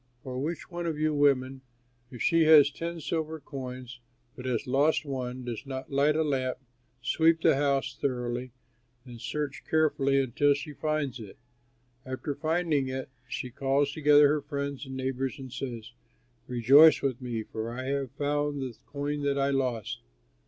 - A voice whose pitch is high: No, medium, 140 Hz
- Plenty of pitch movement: No, narrow, 2.5 semitones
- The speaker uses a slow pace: No, average, 165 wpm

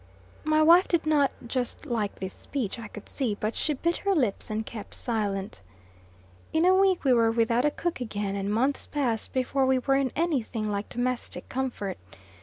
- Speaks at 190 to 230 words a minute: Yes, average, 195 wpm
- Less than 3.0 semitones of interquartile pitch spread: No, wide, 5.4 semitones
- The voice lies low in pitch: No, very high, 250 Hz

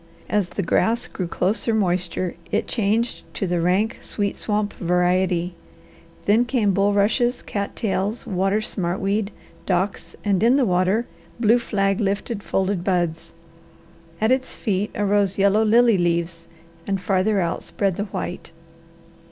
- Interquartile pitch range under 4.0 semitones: Yes, average, 2.9 semitones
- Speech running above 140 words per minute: No, slow, 135 wpm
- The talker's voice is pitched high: Yes, high, 200 Hz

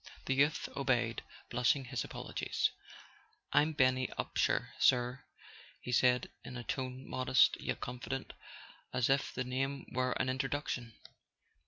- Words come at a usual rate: No, slow, 130 wpm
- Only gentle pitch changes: Yes, narrow, 1.4 semitones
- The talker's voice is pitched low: Yes, low, 130 Hz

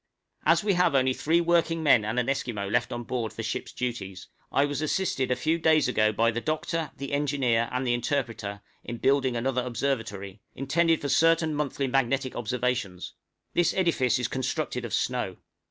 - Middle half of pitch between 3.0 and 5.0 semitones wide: Yes, average, 4.3 semitones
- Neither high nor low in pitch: No, low, 130 Hz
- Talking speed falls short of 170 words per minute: No, average, 180 wpm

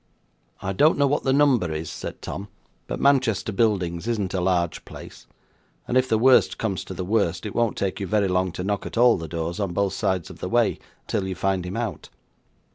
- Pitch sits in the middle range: No, low, 100 Hz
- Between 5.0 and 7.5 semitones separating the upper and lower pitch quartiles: No, average, 4.1 semitones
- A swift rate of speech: Yes, fast, 220 wpm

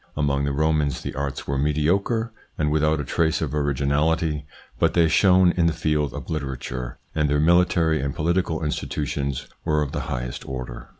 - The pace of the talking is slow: No, average, 175 wpm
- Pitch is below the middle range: Yes, very low, 75 Hz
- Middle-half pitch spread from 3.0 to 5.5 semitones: No, narrow, 2.4 semitones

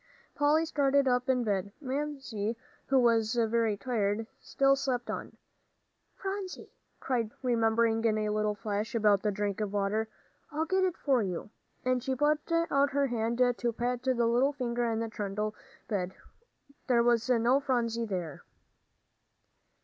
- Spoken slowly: No, average, 150 wpm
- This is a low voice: No, high, 235 Hz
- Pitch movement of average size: Yes, average, 3.9 semitones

